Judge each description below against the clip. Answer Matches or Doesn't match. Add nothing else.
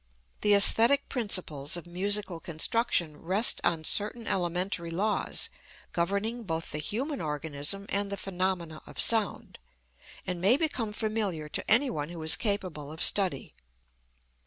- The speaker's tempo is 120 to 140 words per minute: Matches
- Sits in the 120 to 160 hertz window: Doesn't match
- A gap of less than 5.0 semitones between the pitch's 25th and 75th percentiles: Matches